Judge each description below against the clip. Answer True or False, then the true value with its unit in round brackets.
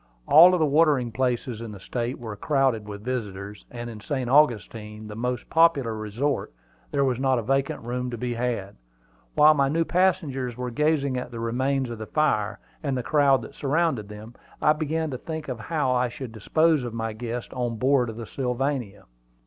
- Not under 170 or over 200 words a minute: True (190 wpm)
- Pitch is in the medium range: False (125 Hz)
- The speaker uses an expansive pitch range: False (3.7 semitones)